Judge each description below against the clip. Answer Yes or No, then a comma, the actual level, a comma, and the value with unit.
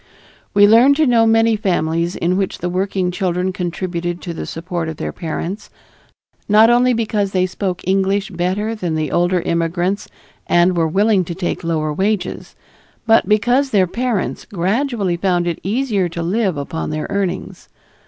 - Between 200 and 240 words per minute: No, average, 165 wpm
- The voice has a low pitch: No, medium, 185 Hz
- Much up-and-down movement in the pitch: No, average, 3.6 semitones